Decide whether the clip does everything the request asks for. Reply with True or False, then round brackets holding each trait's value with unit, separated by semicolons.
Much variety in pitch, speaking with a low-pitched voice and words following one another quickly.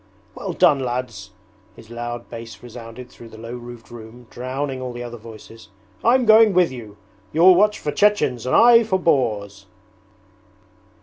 False (6.7 semitones; 125 Hz; 150 wpm)